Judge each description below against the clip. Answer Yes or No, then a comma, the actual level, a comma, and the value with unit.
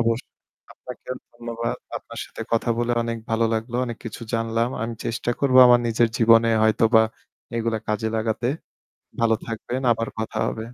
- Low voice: Yes, low, 115 Hz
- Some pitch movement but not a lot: No, narrow, 0.9 semitones